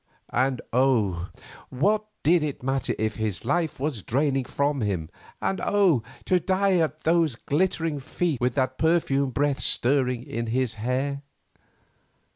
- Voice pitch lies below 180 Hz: Yes, low, 135 Hz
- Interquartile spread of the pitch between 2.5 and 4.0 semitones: No, average, 4.5 semitones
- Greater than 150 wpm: No, average, 140 wpm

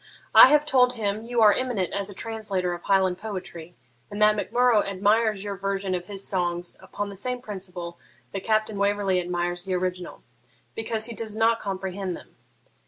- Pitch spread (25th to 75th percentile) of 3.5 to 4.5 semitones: No, average, 3.1 semitones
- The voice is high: Yes, high, 200 Hz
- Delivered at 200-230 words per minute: No, average, 180 wpm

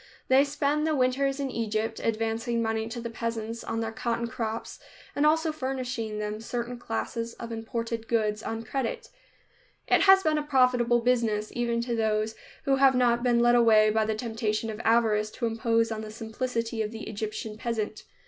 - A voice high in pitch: Yes, high, 230 Hz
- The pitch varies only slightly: Yes, narrow, 2.1 semitones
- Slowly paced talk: No, average, 180 wpm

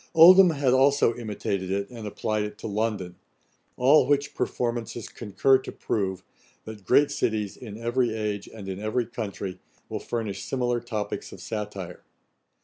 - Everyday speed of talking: Yes, average, 150 wpm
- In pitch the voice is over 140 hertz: No, low, 110 Hz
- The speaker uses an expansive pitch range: No, average, 3.6 semitones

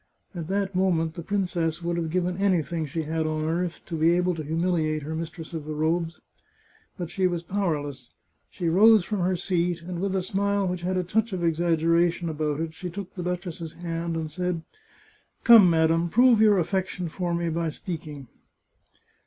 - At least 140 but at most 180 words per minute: No, average, 195 wpm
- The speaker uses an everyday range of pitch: No, narrow, 2.1 semitones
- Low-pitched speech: No, medium, 170 Hz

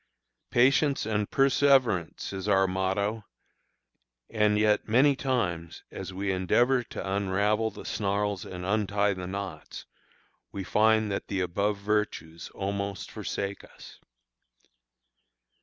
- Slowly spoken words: Yes, slow, 115 wpm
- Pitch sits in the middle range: No, low, 100 Hz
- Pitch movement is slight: Yes, narrow, 2.3 semitones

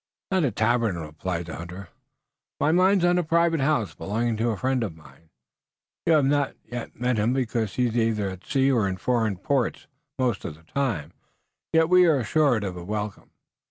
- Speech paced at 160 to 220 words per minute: Yes, average, 190 wpm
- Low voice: Yes, low, 115 Hz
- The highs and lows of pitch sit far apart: Yes, wide, 6.3 semitones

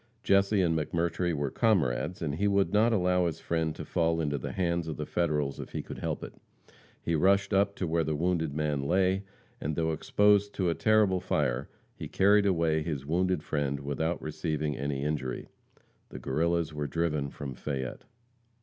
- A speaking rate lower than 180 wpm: No, average, 185 wpm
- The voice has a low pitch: Yes, very low, 80 Hz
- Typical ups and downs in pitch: Yes, average, 3.8 semitones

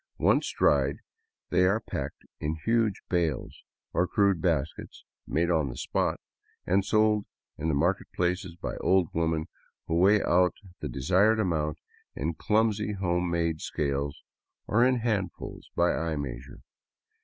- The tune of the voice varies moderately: Yes, average, 4.3 semitones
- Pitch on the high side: No, very low, 85 Hz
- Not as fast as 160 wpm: Yes, average, 140 wpm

